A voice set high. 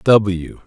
No: low, 100 Hz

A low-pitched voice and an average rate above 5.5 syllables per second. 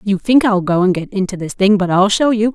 No: high, 200 Hz; 5.7 syllables/s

